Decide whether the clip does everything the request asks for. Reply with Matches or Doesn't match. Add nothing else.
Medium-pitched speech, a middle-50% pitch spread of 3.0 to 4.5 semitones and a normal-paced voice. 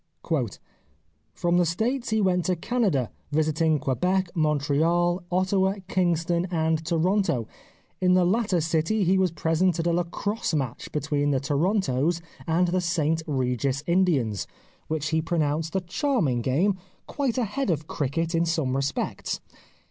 Matches